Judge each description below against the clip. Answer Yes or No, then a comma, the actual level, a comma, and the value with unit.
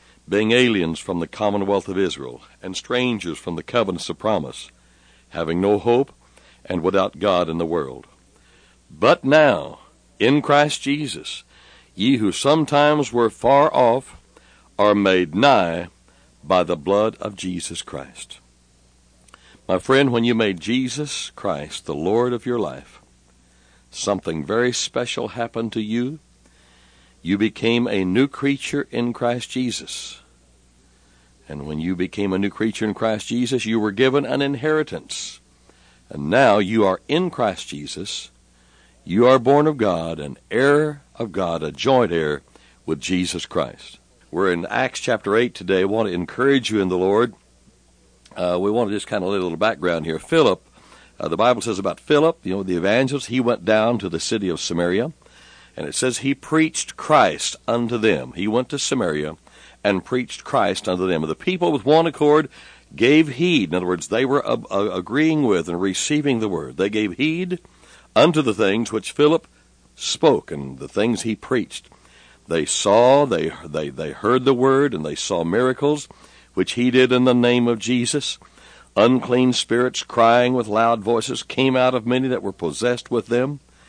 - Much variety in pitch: Yes, wide, 7.3 semitones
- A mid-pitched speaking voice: No, low, 110 Hz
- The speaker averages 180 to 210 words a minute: No, average, 170 wpm